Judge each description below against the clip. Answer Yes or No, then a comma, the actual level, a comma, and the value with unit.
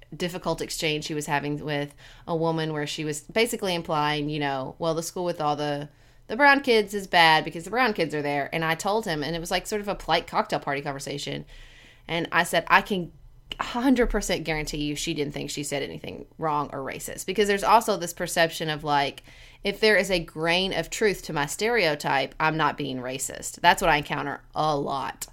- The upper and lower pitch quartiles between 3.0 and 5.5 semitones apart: Yes, average, 3.9 semitones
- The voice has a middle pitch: Yes, medium, 160 Hz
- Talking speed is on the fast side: Yes, fast, 215 wpm